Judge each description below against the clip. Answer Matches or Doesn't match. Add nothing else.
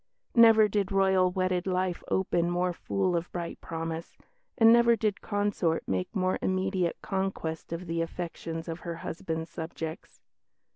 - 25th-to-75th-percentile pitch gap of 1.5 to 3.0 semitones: Matches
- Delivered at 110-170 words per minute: Matches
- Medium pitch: Matches